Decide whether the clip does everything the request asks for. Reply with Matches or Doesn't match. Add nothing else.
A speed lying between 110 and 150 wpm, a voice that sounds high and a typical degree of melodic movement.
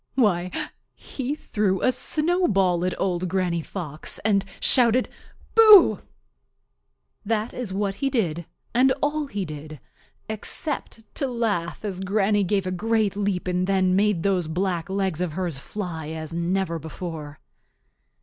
Matches